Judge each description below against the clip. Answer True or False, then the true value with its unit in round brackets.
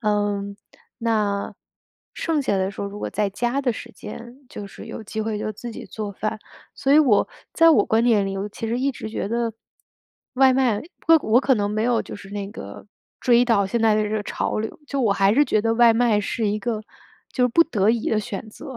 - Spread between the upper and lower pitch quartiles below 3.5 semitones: True (2.8 semitones)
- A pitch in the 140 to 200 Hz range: False (220 Hz)